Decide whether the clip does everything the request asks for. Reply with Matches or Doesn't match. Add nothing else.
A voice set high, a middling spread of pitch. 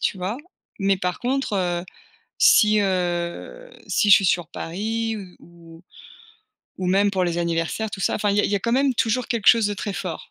Matches